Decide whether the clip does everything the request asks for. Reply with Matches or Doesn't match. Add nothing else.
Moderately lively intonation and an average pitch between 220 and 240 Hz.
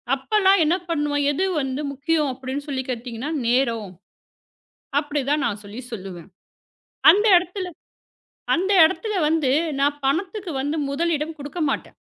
Doesn't match